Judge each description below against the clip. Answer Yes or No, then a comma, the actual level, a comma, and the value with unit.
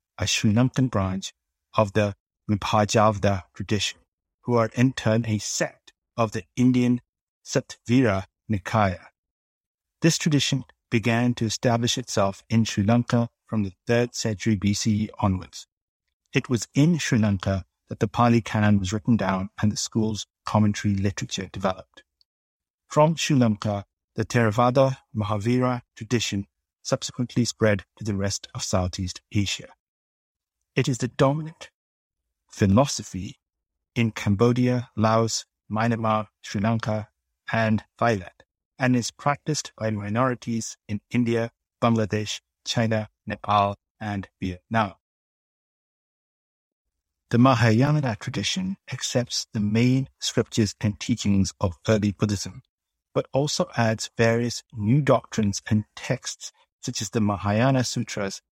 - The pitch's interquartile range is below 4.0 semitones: Yes, average, 3.2 semitones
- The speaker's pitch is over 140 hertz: No, low, 110 Hz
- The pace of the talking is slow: Yes, slow, 120 wpm